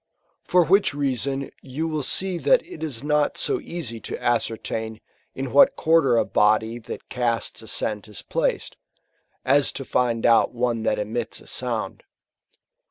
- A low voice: Yes, low, 130 Hz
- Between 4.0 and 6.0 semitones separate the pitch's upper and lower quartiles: Yes, wide, 5.4 semitones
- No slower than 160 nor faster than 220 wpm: No, average, 145 wpm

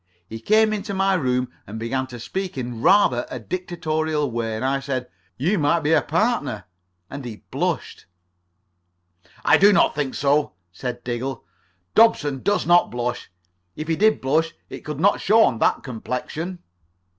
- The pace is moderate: Yes, average, 165 wpm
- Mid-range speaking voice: Yes, medium, 145 Hz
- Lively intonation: Yes, wide, 6.6 semitones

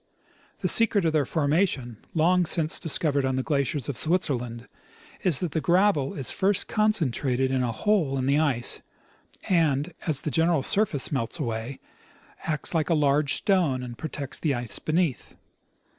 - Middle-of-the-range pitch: Yes, medium, 150 Hz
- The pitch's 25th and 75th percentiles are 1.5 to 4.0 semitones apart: No, average, 4.4 semitones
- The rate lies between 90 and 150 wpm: No, average, 160 wpm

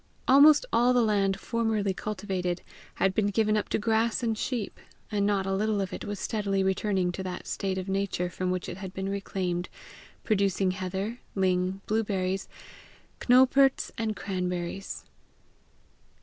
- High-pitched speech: Yes, high, 195 Hz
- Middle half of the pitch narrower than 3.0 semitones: Yes, narrow, 2.5 semitones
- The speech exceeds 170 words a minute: No, average, 150 wpm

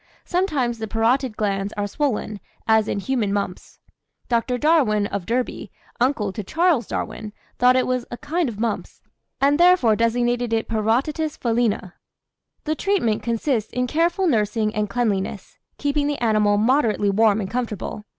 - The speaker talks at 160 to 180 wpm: No, average, 150 wpm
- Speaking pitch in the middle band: No, high, 235 Hz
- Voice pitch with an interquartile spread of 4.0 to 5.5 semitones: Yes, average, 4.4 semitones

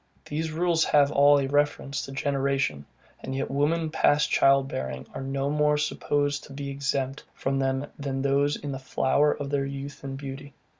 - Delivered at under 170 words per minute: No, average, 185 wpm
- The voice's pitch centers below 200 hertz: Yes, medium, 140 Hz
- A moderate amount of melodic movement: No, narrow, 1.2 semitones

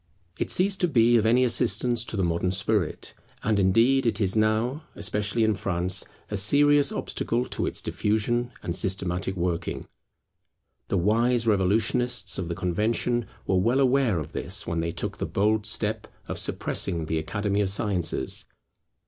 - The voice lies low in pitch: Yes, low, 105 Hz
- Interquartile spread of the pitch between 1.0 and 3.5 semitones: No, average, 4.2 semitones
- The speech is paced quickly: No, average, 160 wpm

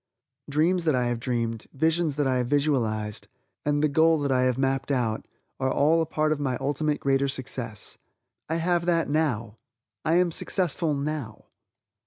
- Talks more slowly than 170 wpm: No, average, 175 wpm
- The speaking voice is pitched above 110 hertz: Yes, medium, 140 Hz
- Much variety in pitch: No, average, 3.8 semitones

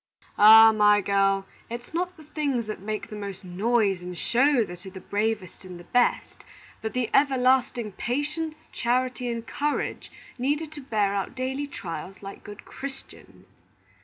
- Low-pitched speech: No, high, 230 Hz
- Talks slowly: No, average, 160 wpm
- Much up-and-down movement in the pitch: No, average, 5.0 semitones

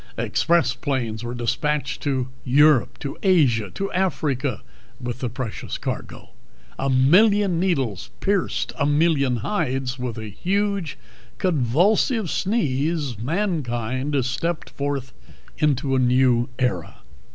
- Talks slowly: Yes, slow, 120 wpm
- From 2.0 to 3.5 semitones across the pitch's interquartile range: No, wide, 5.4 semitones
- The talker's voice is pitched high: No, low, 135 Hz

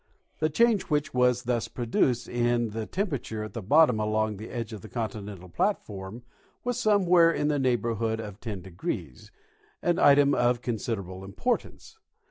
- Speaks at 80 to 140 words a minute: No, average, 155 wpm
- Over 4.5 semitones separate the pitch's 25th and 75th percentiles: Yes, wide, 5.4 semitones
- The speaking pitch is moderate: No, low, 120 Hz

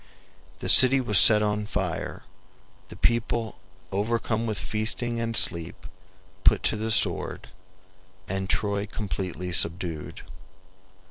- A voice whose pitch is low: Yes, low, 105 Hz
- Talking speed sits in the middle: No, slow, 115 wpm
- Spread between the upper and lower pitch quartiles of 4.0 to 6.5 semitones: No, average, 3.1 semitones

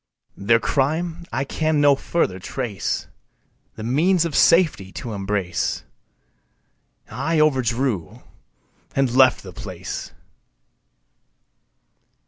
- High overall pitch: No, low, 130 Hz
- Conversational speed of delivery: No, slow, 95 wpm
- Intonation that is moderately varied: No, wide, 6.9 semitones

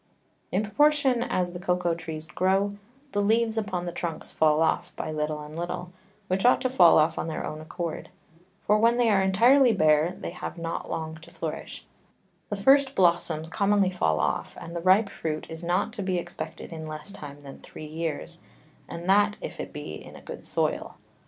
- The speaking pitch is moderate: Yes, medium, 180 Hz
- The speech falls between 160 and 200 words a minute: Yes, average, 195 wpm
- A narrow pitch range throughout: No, average, 4.2 semitones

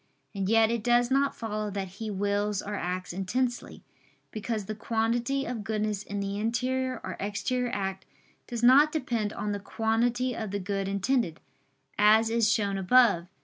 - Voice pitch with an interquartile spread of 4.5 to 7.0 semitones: No, average, 3.1 semitones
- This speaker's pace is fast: No, average, 165 wpm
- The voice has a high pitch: Yes, high, 215 Hz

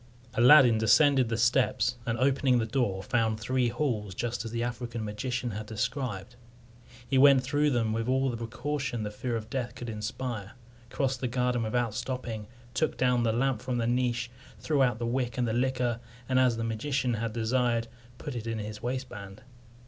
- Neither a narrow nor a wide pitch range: No, narrow, 2.3 semitones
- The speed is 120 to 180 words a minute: No, average, 190 wpm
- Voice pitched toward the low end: Yes, low, 120 Hz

